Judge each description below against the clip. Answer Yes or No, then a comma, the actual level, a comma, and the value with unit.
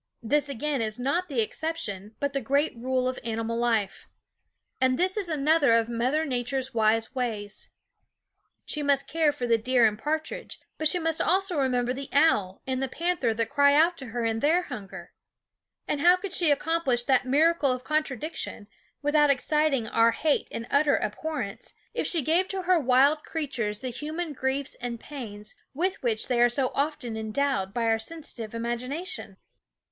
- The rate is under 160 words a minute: No, average, 175 wpm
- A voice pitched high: Yes, very high, 265 Hz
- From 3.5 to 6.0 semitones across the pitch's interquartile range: Yes, average, 4.9 semitones